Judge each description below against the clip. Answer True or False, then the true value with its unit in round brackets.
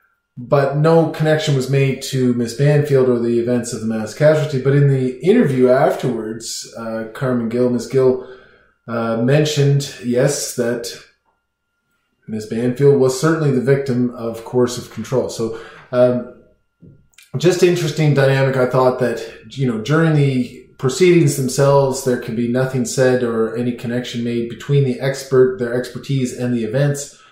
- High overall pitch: False (130 Hz)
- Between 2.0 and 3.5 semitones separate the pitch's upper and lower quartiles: True (2.6 semitones)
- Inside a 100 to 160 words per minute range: True (155 wpm)